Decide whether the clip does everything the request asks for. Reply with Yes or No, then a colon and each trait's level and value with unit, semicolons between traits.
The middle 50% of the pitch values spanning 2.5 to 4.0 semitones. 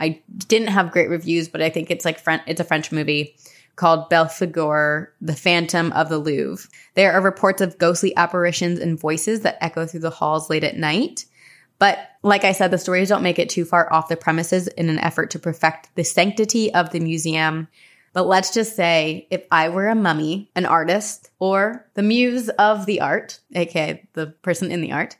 Yes: average, 3.1 semitones